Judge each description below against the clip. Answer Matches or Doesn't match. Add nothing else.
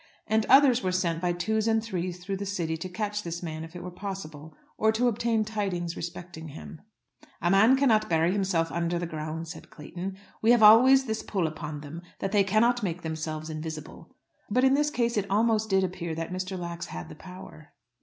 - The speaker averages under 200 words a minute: Doesn't match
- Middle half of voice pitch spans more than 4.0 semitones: Matches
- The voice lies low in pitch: Doesn't match